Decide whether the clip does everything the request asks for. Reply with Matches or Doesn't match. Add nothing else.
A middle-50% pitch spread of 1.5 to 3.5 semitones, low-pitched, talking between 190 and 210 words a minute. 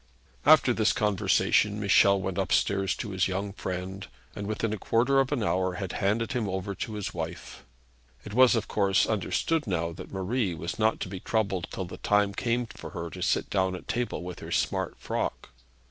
Matches